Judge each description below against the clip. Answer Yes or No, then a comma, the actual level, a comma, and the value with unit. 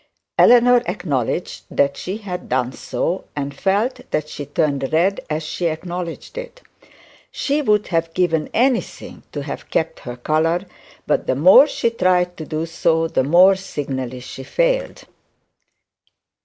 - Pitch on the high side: No, medium, 170 Hz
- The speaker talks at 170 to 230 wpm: No, average, 145 wpm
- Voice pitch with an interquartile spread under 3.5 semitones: No, average, 5.1 semitones